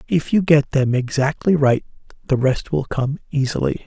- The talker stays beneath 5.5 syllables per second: Yes, 4.9 syllables/s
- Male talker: Yes, male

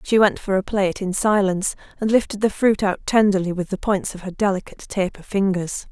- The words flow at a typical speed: No, fast, 215 wpm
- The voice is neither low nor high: No, high, 195 Hz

